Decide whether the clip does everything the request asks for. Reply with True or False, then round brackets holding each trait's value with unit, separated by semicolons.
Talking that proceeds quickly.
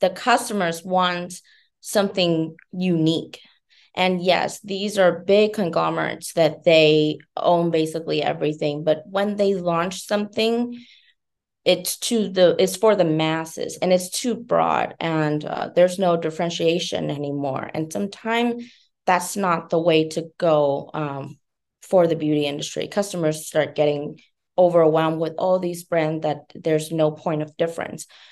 False (140 wpm)